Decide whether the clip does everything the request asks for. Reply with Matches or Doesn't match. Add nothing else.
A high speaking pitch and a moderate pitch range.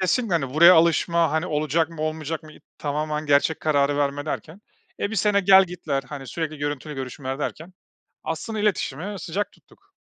Doesn't match